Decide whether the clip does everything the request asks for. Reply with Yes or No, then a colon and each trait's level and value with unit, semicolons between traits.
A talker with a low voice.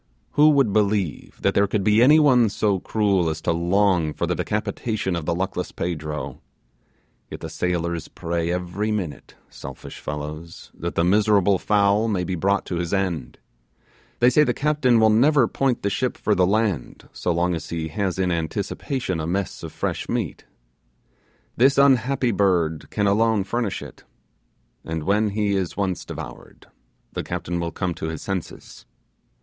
Yes: very low, 95 Hz